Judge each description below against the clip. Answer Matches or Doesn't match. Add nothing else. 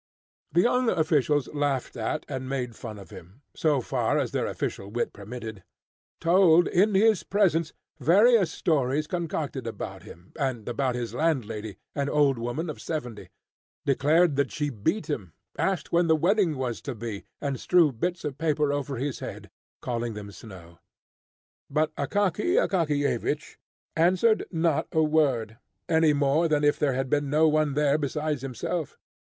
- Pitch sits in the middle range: Matches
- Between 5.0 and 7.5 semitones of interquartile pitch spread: Doesn't match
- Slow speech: Doesn't match